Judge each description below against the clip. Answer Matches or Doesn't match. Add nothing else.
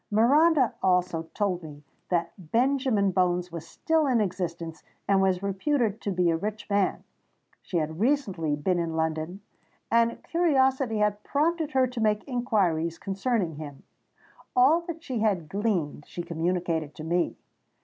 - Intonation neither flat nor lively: Doesn't match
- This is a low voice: Doesn't match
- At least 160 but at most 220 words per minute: Doesn't match